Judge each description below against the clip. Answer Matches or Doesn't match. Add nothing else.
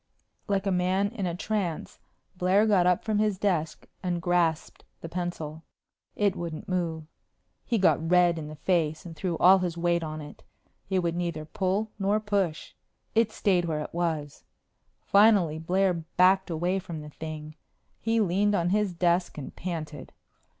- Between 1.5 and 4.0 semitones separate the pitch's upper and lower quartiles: Matches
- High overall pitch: Doesn't match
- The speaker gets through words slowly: Doesn't match